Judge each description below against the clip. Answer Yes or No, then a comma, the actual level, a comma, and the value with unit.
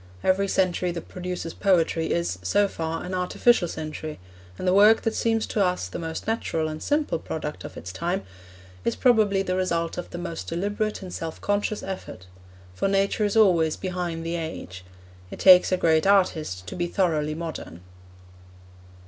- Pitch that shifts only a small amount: No, average, 3.5 semitones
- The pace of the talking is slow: No, average, 175 wpm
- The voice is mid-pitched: Yes, medium, 180 Hz